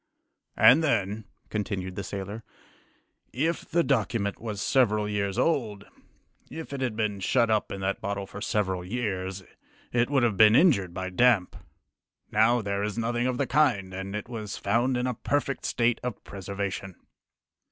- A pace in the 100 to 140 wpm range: No, average, 165 wpm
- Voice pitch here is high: No, low, 105 Hz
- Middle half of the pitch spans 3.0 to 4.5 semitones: Yes, average, 3.8 semitones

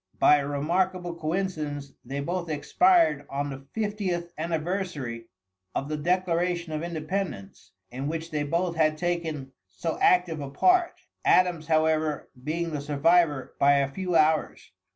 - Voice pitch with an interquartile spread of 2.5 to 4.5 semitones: Yes, average, 3.5 semitones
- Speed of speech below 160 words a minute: Yes, average, 140 wpm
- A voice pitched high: No, medium, 160 Hz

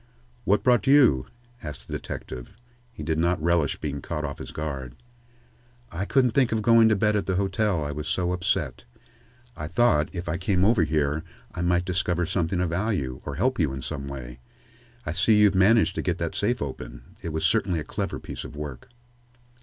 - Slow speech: No, average, 200 wpm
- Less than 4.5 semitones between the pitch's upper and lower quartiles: No, wide, 5.4 semitones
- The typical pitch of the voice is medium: No, very low, 85 Hz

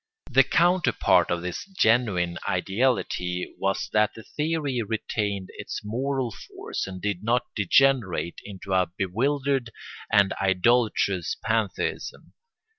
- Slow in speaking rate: Yes, slow, 115 wpm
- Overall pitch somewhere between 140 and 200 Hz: No, low, 105 Hz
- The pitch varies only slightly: No, wide, 5.5 semitones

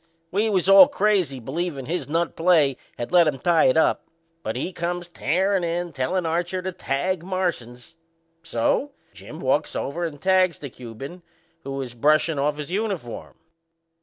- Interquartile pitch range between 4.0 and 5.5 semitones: Yes, average, 4.9 semitones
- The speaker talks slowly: No, average, 165 wpm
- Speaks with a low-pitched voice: No, medium, 170 Hz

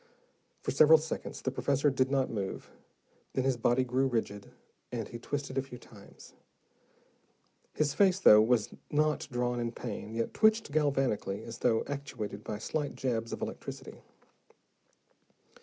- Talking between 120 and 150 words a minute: Yes, average, 140 wpm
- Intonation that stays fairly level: No, average, 3.8 semitones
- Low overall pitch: Yes, low, 130 Hz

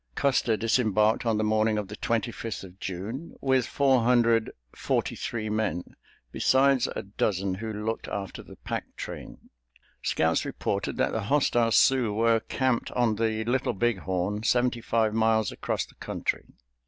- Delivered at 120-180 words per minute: Yes, average, 160 wpm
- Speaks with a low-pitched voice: Yes, low, 110 Hz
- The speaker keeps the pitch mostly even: Yes, narrow, 2.2 semitones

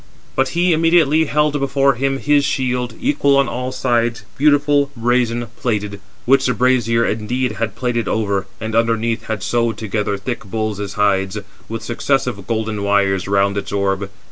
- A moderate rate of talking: Yes, average, 155 wpm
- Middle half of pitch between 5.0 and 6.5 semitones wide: No, average, 4.4 semitones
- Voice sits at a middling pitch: No, low, 115 Hz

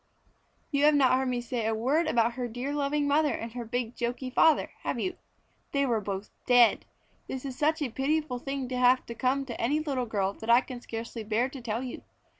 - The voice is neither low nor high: No, very high, 255 Hz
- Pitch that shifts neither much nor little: Yes, average, 3.0 semitones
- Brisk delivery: Yes, fast, 220 wpm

